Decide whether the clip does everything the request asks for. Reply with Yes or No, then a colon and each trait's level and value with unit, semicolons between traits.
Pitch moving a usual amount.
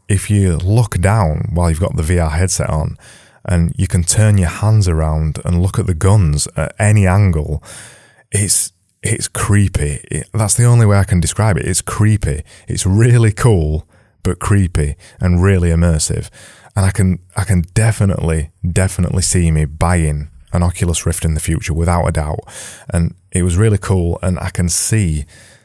Yes: average, 3.9 semitones